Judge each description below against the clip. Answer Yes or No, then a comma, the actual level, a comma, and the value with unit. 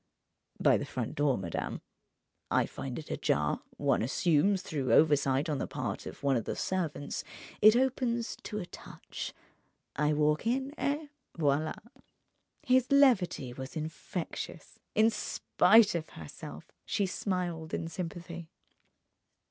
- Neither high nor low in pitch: Yes, medium, 170 Hz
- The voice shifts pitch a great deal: Yes, wide, 6.7 semitones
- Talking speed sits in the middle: No, slow, 125 wpm